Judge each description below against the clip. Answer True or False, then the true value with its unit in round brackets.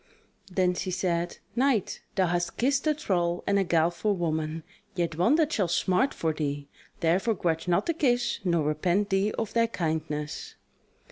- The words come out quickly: False (165 wpm)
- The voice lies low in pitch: False (180 Hz)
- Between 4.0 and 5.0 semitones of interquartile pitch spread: True (4.5 semitones)